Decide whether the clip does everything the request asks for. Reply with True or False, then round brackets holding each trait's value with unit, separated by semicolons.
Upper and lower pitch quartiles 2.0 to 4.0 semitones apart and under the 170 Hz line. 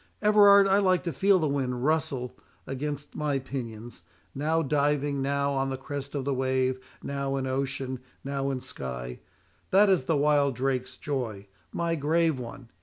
True (2.5 semitones; 140 Hz)